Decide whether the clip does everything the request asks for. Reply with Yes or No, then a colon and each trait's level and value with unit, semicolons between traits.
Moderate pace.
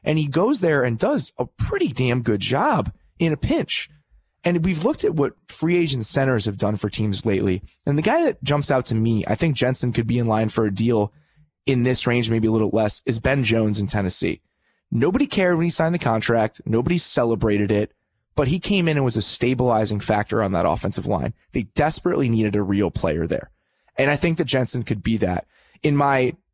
No: fast, 220 wpm